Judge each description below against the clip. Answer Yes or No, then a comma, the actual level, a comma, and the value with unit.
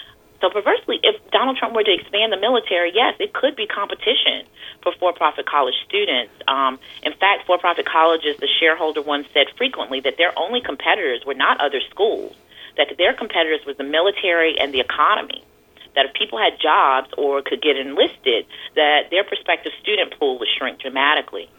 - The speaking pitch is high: Yes, high, 210 Hz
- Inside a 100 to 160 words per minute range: No, average, 175 wpm